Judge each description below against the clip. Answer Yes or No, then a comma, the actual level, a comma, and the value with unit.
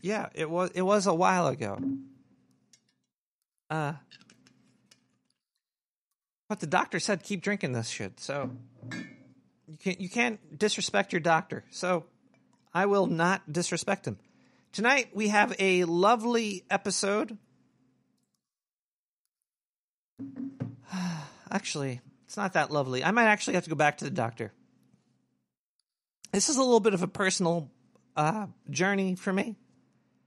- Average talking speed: No, slow, 125 wpm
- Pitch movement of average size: No, wide, 5.9 semitones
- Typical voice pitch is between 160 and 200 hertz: Yes, medium, 185 Hz